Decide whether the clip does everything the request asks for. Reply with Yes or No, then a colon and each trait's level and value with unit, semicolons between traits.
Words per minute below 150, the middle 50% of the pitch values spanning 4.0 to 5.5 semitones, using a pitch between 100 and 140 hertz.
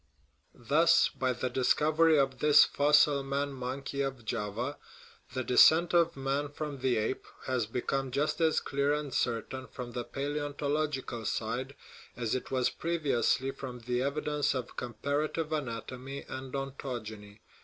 No: average, 140 wpm; average, 2.8 semitones; low, 135 Hz